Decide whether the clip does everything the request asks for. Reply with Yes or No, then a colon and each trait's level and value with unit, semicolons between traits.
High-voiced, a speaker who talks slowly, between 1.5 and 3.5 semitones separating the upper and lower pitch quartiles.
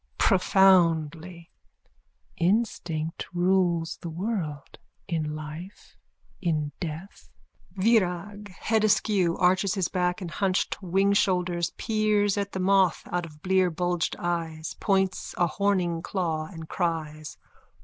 No: medium, 180 Hz; slow, 110 wpm; average, 2.8 semitones